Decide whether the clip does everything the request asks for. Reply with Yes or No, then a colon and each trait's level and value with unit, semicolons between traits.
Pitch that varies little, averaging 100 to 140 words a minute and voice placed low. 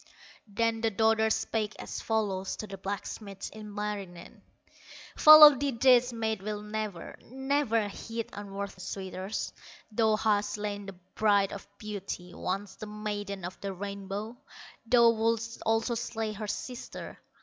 No: narrow, 2.2 semitones; slow, 135 wpm; high, 210 Hz